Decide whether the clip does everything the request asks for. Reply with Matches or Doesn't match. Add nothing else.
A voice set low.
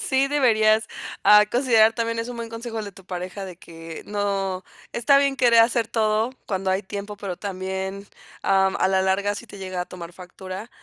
Doesn't match